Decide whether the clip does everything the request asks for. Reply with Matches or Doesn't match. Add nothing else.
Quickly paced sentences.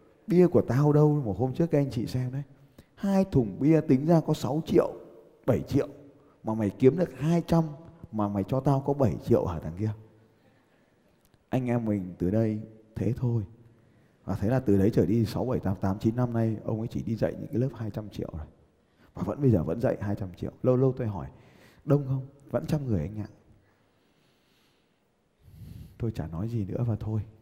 Doesn't match